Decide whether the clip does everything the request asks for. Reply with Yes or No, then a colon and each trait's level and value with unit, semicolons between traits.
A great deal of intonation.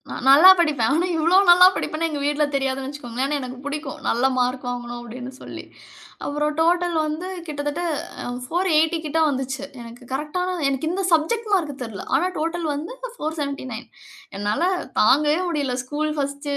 No: average, 3.6 semitones